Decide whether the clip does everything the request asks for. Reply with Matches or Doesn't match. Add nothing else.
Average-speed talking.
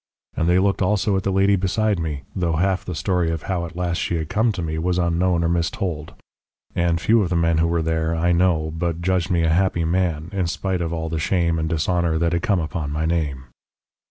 Doesn't match